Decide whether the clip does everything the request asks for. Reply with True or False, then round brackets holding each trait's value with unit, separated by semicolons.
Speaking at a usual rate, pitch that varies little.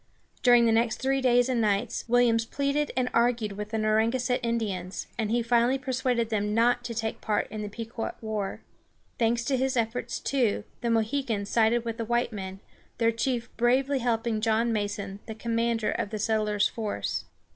True (180 wpm; 2.0 semitones)